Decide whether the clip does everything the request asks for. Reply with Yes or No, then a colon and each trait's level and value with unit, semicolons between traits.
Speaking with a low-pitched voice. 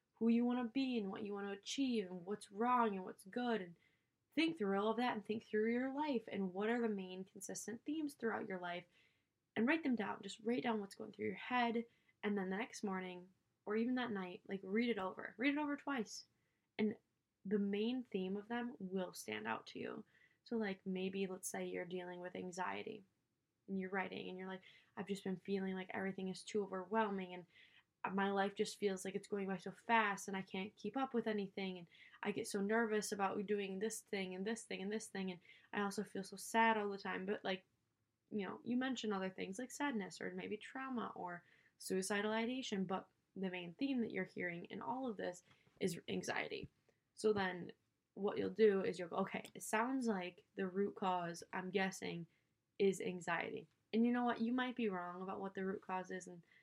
No: high, 200 Hz